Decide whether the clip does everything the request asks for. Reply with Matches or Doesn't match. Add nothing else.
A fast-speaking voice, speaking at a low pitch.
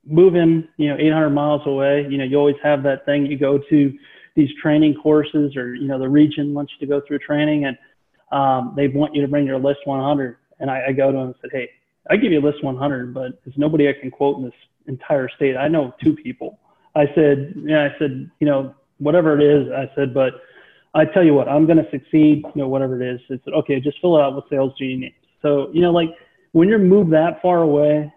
Doesn't match